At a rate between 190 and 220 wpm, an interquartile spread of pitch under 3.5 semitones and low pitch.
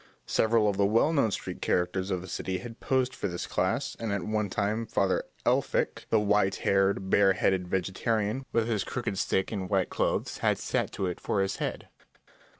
Yes: average, 195 wpm; average, 2.7 semitones; low, 100 Hz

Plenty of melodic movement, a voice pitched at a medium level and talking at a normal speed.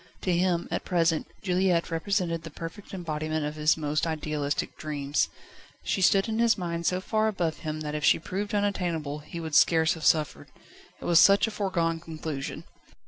No: average, 3.3 semitones; medium, 165 Hz; average, 180 wpm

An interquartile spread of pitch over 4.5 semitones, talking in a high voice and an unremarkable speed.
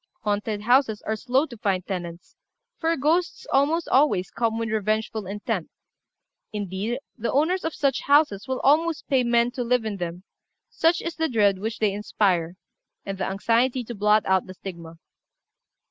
Yes: average, 5.2 semitones; high, 220 Hz; average, 165 wpm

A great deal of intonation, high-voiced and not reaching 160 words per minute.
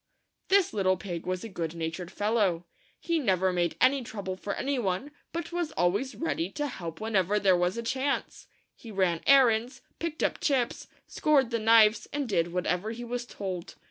No: wide, 6.3 semitones; high, 215 Hz; average, 185 wpm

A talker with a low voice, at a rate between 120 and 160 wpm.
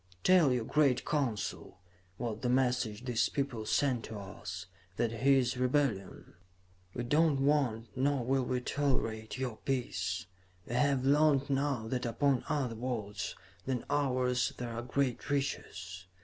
Yes: low, 125 Hz; average, 150 wpm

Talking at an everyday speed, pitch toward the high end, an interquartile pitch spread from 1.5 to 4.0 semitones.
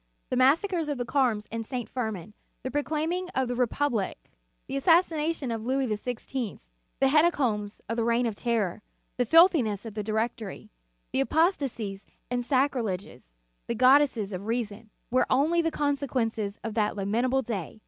No: average, 160 wpm; high, 245 Hz; average, 4.5 semitones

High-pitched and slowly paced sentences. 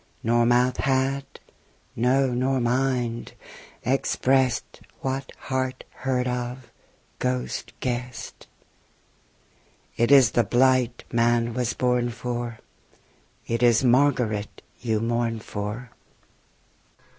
No: low, 125 Hz; slow, 95 wpm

